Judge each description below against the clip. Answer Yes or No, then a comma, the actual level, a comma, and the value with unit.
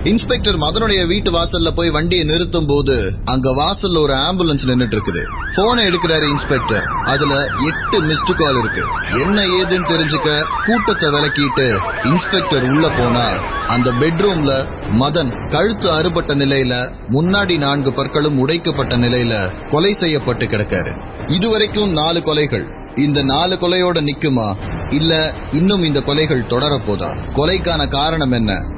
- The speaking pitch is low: No, medium, 150 Hz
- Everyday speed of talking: No, slow, 120 wpm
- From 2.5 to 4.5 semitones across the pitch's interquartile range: No, wide, 5.4 semitones